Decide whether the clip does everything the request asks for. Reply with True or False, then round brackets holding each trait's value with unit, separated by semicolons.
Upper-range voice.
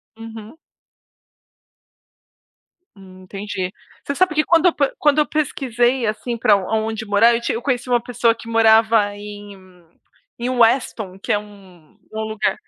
True (225 Hz)